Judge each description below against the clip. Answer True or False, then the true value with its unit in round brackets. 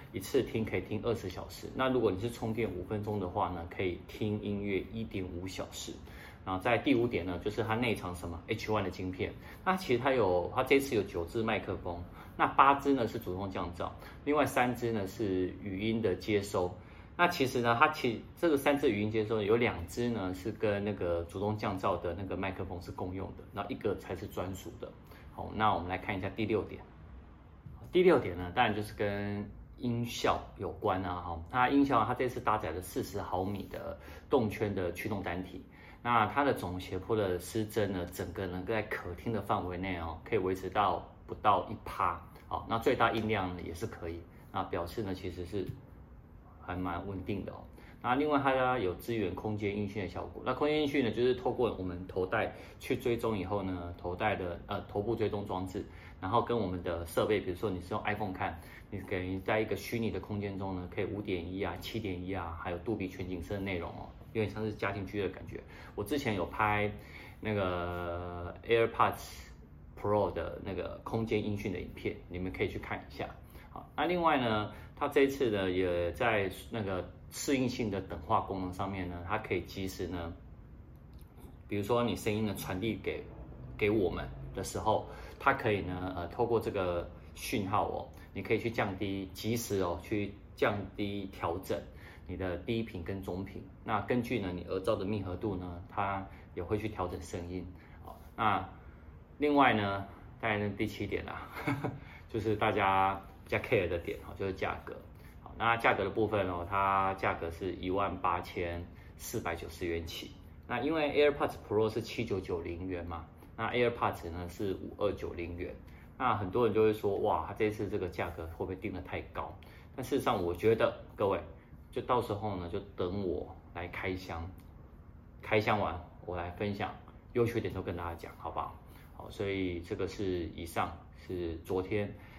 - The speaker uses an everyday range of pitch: True (3.6 semitones)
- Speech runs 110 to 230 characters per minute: False (285 characters per minute)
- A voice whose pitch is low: True (95 Hz)